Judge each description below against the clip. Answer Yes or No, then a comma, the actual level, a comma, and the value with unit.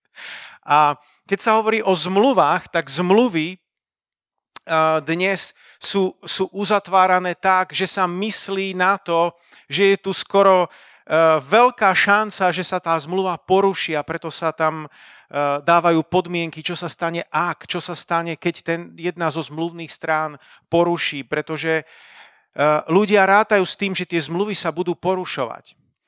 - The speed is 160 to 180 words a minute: No, average, 140 wpm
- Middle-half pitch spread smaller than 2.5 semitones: No, average, 2.9 semitones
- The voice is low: No, medium, 175 Hz